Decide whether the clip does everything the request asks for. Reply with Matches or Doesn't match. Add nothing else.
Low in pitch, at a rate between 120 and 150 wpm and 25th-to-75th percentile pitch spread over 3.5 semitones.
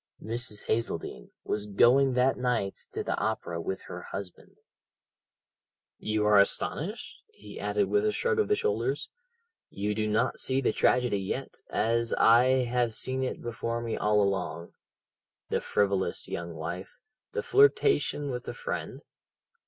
Matches